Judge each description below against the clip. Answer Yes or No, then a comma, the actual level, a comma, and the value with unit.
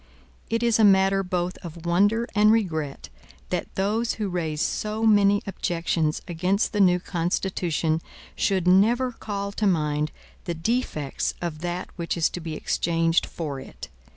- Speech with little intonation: No, average, 3.7 semitones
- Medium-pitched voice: Yes, medium, 180 Hz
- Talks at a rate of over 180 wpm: No, average, 155 wpm